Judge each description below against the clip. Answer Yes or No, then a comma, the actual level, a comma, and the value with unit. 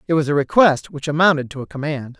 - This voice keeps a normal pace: No, fast, 245 wpm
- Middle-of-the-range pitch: Yes, medium, 150 Hz